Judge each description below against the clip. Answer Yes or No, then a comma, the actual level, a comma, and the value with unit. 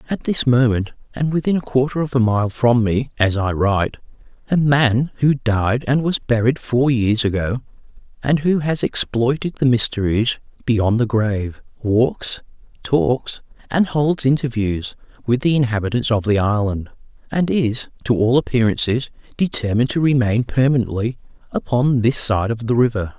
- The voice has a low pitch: Yes, low, 120 Hz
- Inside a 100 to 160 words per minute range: Yes, average, 155 wpm